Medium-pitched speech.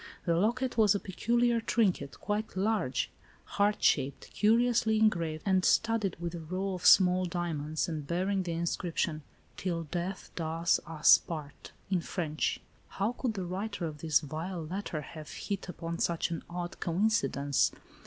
Yes: medium, 180 Hz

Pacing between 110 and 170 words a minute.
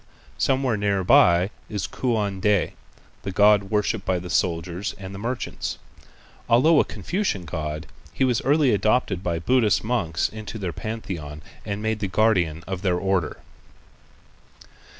Yes: average, 140 wpm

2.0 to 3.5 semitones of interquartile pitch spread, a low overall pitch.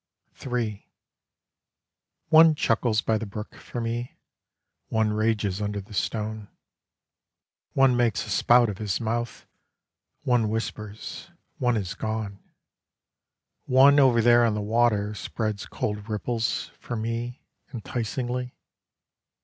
Yes: narrow, 2.4 semitones; low, 110 Hz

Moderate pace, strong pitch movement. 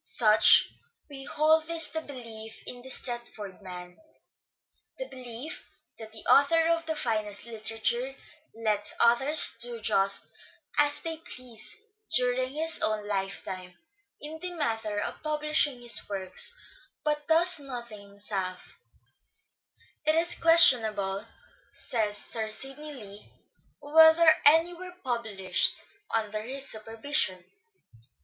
No: slow, 125 wpm; wide, 6.1 semitones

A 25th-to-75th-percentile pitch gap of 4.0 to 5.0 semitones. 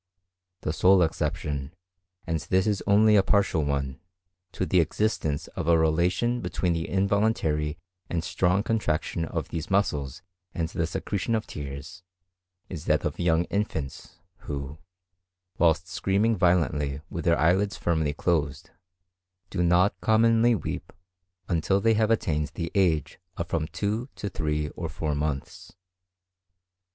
Yes: average, 4.5 semitones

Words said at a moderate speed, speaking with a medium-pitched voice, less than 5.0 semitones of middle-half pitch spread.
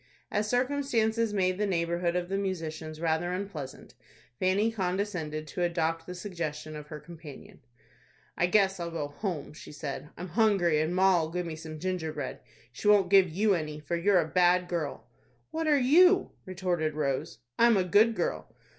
Yes: average, 170 wpm; medium, 180 Hz; average, 4.1 semitones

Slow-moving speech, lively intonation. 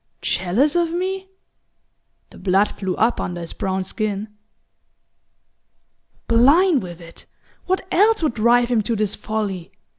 Yes: slow, 130 wpm; wide, 8.2 semitones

